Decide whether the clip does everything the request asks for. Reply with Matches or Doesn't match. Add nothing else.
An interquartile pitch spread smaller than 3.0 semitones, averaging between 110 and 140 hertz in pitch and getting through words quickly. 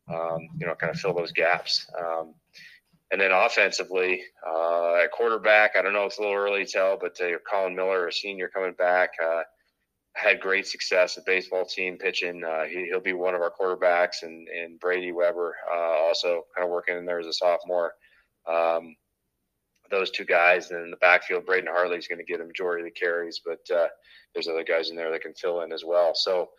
Doesn't match